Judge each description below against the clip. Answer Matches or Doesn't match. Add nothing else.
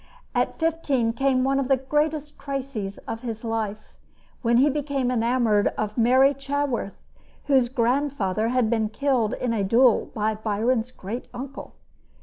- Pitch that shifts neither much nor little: Matches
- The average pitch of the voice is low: Doesn't match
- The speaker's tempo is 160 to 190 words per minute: Doesn't match